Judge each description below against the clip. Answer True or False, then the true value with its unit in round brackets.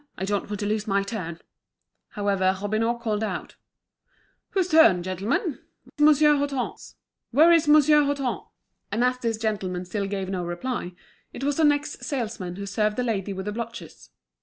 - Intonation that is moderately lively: False (6.0 semitones)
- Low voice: False (220 Hz)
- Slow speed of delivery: False (160 wpm)